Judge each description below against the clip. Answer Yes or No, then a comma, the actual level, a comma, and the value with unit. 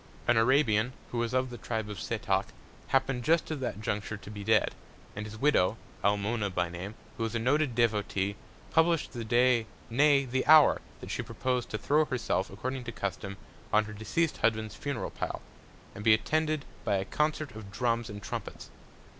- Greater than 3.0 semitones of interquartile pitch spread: Yes, average, 4.1 semitones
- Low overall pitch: Yes, low, 115 Hz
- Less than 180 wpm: No, average, 185 wpm